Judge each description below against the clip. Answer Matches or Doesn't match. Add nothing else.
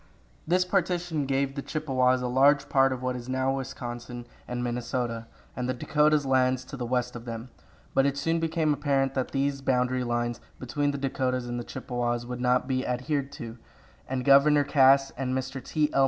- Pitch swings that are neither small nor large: Doesn't match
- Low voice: Matches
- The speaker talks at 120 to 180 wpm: Doesn't match